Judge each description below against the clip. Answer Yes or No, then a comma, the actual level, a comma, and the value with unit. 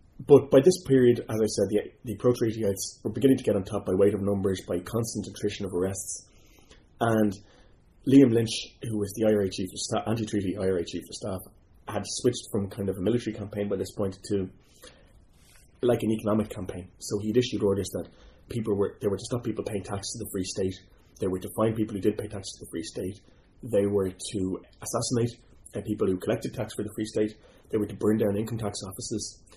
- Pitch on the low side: Yes, low, 105 Hz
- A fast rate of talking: Yes, fast, 215 wpm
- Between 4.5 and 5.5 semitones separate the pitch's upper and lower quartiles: No, narrow, 2.5 semitones